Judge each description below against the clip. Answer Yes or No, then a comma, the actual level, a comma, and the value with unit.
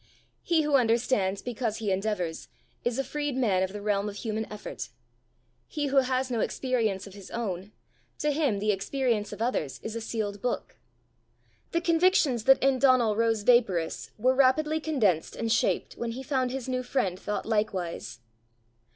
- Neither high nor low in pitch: No, high, 230 Hz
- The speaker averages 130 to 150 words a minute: No, average, 170 wpm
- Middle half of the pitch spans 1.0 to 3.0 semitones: No, average, 4.3 semitones